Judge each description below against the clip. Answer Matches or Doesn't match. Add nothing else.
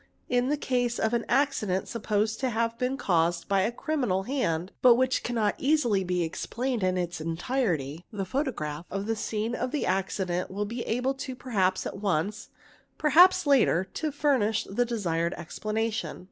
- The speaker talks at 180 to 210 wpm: Doesn't match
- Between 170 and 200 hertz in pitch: Doesn't match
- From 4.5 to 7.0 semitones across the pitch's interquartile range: Matches